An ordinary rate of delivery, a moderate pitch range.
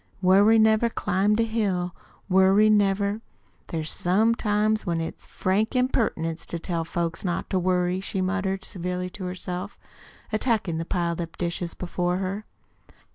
Yes: average, 145 wpm; average, 3.0 semitones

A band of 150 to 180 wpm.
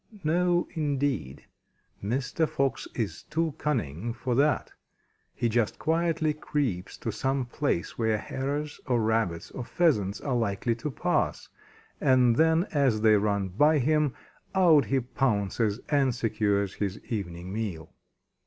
No: slow, 135 wpm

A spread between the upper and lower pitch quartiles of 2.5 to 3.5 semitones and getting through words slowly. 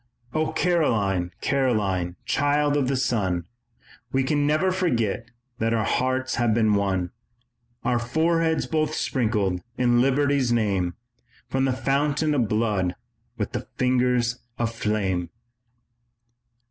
No: average, 5.2 semitones; slow, 120 wpm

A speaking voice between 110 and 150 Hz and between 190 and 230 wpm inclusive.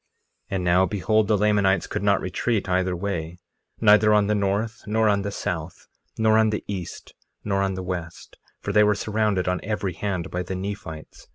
No: low, 100 Hz; average, 195 wpm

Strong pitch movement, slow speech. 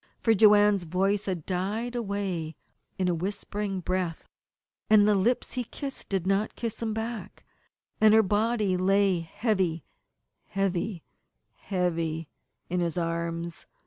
No: average, 3.3 semitones; slow, 130 wpm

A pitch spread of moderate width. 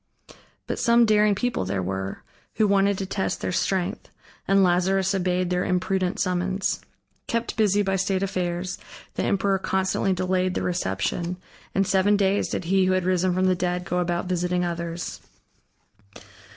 No: narrow, 1.6 semitones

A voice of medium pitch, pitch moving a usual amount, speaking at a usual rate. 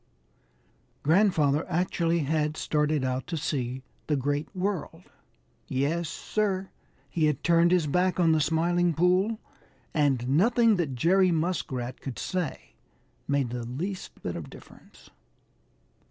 No: medium, 160 Hz; average, 4.1 semitones; slow, 125 wpm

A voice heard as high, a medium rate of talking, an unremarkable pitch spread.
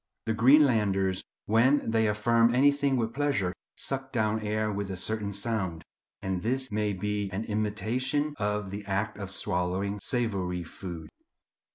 No: low, 105 Hz; average, 145 wpm; average, 3.3 semitones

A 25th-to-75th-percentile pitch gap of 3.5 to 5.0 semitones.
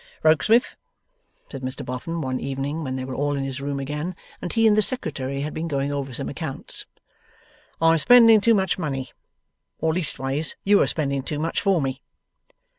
Yes: average, 3.8 semitones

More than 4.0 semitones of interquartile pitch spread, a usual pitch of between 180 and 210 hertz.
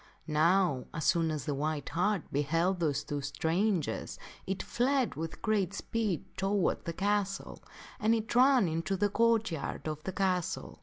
Yes: average, 4.7 semitones; medium, 185 Hz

